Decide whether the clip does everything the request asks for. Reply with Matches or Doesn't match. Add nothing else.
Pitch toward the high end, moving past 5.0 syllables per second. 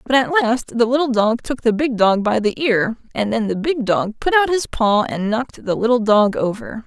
Doesn't match